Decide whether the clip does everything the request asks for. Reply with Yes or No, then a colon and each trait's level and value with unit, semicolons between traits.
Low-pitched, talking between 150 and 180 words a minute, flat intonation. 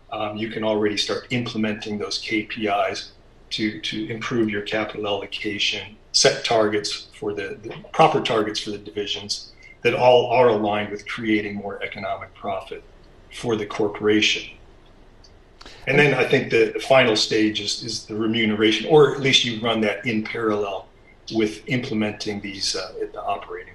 Yes: low, 110 Hz; average, 160 wpm; narrow, 1.3 semitones